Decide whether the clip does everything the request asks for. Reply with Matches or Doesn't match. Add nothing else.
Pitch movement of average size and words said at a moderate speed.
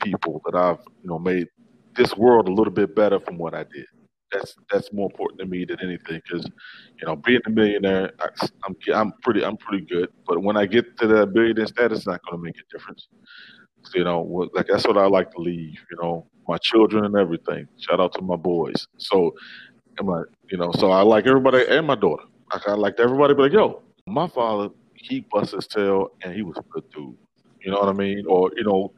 Doesn't match